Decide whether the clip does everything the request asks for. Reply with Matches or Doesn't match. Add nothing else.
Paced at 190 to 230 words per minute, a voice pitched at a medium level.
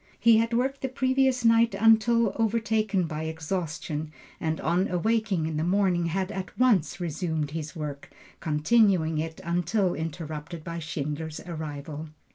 Doesn't match